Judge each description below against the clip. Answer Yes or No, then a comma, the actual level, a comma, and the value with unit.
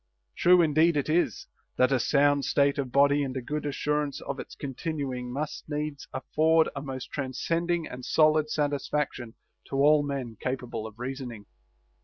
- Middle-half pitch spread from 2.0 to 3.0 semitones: Yes, average, 2.7 semitones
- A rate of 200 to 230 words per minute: No, average, 165 wpm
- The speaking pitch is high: No, medium, 140 Hz